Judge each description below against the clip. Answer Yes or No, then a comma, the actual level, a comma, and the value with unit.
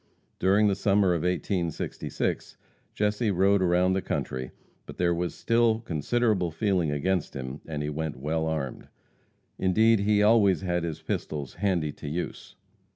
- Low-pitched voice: Yes, very low, 90 Hz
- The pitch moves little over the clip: No, average, 4.3 semitones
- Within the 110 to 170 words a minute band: Yes, average, 150 wpm